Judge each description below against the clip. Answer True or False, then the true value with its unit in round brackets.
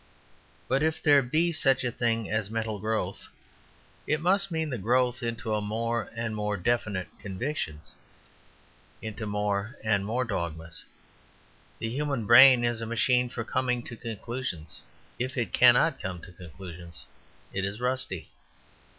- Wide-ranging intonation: False (3.7 semitones)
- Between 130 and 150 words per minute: True (140 wpm)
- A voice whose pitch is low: True (115 Hz)